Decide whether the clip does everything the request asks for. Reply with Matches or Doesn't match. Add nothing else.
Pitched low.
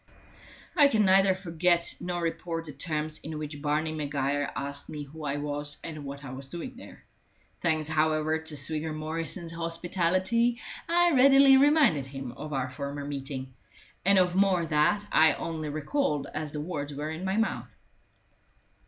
Doesn't match